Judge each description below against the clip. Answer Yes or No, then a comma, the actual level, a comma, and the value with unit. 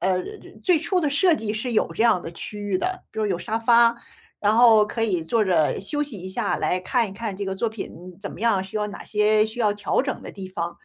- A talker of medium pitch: No, high, 210 Hz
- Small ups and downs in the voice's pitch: No, average, 3.6 semitones